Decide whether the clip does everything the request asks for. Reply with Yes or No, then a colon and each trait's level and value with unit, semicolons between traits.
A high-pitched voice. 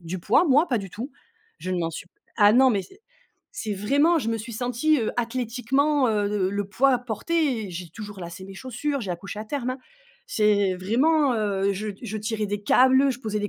Yes: high, 220 Hz